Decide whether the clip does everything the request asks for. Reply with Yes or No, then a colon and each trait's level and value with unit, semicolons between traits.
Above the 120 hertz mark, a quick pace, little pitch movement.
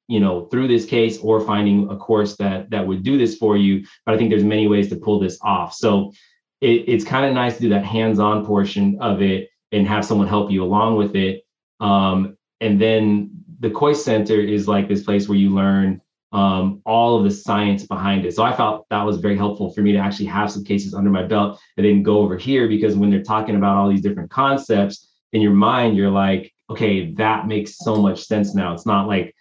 No: low, 105 Hz; fast, 230 wpm; narrow, 1.7 semitones